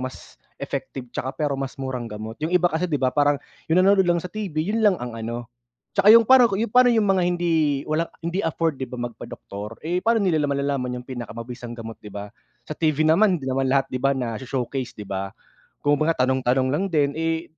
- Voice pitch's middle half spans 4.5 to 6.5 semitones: Yes, wide, 5.6 semitones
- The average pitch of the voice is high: No, medium, 145 Hz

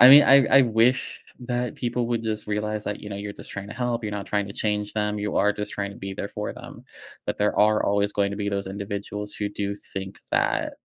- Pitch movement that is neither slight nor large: No, narrow, 1.6 semitones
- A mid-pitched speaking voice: No, low, 105 Hz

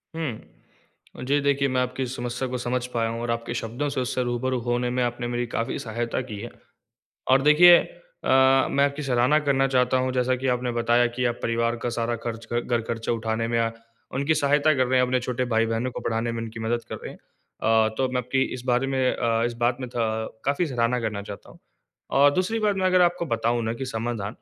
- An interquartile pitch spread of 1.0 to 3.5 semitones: Yes, narrow, 2.4 semitones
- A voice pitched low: Yes, low, 125 Hz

